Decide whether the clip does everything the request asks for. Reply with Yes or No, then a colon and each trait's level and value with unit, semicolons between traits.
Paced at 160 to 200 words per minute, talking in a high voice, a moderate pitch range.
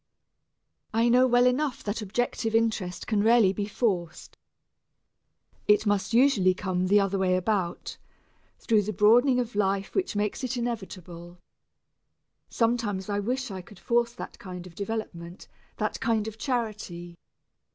No: average, 140 wpm; high, 210 Hz; average, 3.9 semitones